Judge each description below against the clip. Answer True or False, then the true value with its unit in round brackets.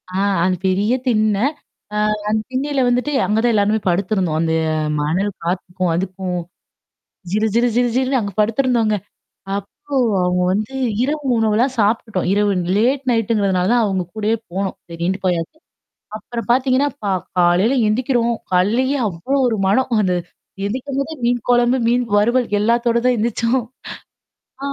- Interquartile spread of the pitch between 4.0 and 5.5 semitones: True (4.3 semitones)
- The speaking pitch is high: True (220 Hz)